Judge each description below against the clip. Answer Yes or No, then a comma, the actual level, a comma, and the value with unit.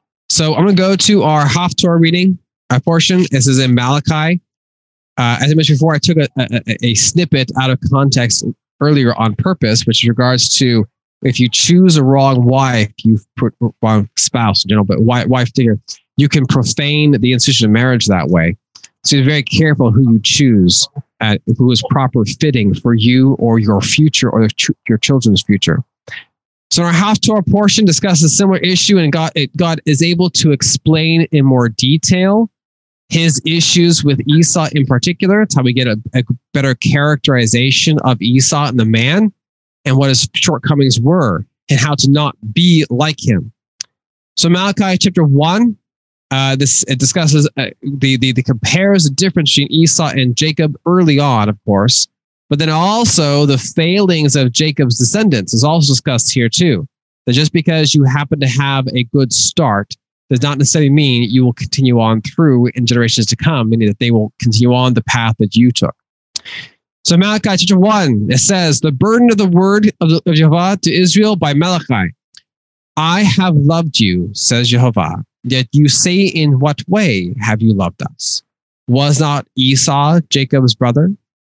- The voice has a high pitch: No, medium, 140 Hz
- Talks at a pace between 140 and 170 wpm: No, average, 180 wpm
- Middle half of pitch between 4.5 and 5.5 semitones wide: Yes, average, 5.0 semitones